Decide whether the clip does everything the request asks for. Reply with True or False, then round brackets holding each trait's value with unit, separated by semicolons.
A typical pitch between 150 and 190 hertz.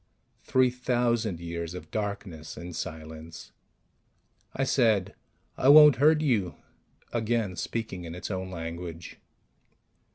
False (100 Hz)